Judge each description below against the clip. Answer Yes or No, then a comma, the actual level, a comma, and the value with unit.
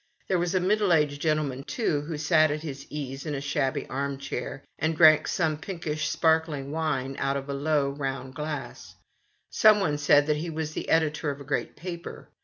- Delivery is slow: No, fast, 205 wpm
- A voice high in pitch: No, medium, 150 Hz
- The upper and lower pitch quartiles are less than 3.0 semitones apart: Yes, narrow, 2.4 semitones